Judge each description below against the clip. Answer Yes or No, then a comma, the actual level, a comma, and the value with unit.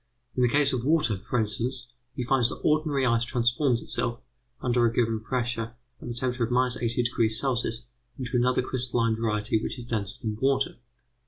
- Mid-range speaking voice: No, low, 120 Hz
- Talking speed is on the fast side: No, average, 175 wpm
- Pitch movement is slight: Yes, narrow, 1.9 semitones